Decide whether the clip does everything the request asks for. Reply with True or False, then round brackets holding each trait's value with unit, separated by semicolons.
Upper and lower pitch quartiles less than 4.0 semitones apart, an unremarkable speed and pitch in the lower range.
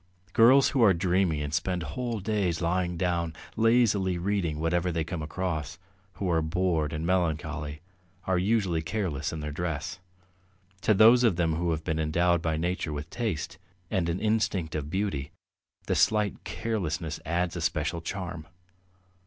True (3.4 semitones; 160 wpm; 85 Hz)